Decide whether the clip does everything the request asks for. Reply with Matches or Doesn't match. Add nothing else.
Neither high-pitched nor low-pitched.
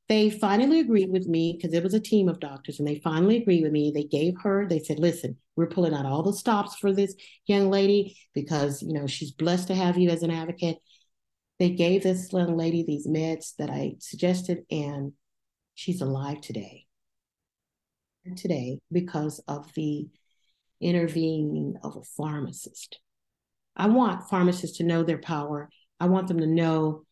Matches